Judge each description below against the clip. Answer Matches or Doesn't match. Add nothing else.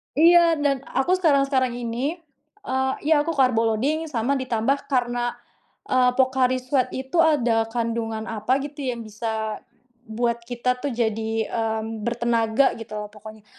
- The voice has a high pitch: Matches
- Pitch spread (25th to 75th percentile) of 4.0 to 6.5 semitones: Doesn't match